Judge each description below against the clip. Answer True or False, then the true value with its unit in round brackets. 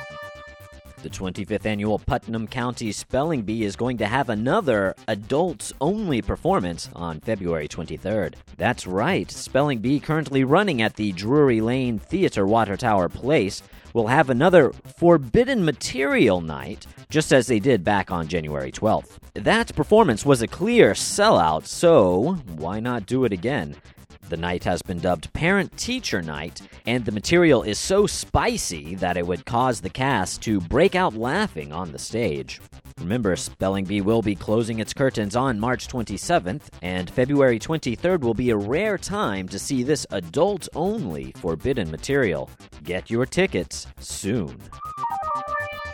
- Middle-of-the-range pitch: False (110 Hz)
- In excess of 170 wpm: False (150 wpm)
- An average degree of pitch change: False (7.6 semitones)